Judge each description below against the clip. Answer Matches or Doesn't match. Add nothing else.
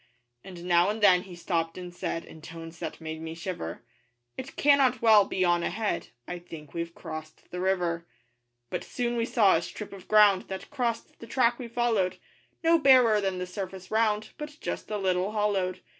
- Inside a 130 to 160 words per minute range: Doesn't match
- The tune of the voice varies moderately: Matches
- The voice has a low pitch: Doesn't match